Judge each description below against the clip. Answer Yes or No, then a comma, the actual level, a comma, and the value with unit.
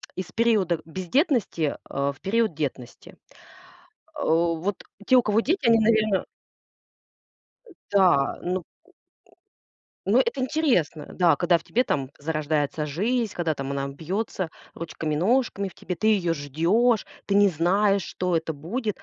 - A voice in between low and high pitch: Yes, medium, 180 Hz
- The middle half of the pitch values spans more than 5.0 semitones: Yes, wide, 5.6 semitones